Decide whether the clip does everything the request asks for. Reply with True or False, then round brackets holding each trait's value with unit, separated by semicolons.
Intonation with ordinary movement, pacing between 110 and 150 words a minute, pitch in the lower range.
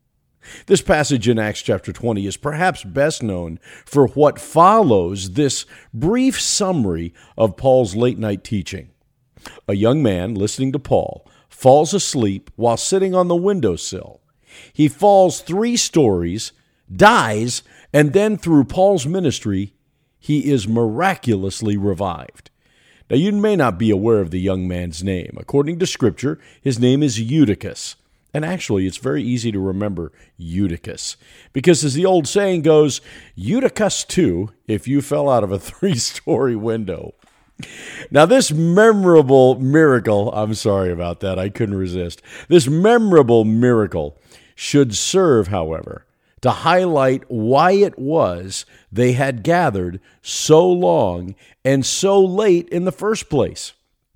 False (8.1 semitones; 135 wpm; 130 Hz)